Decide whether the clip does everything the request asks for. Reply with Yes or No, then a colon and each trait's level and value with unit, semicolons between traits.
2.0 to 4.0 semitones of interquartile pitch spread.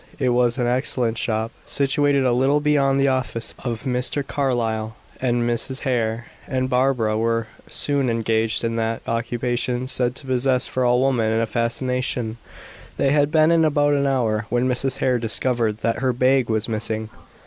Yes: average, 2.7 semitones